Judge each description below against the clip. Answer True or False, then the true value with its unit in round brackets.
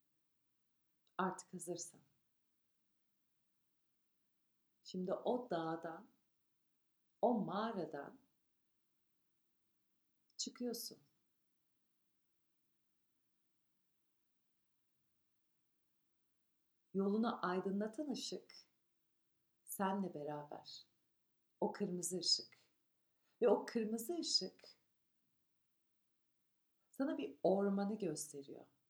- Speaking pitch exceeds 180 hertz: True (190 Hz)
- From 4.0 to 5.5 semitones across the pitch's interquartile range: True (5.1 semitones)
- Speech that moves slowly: True (50 wpm)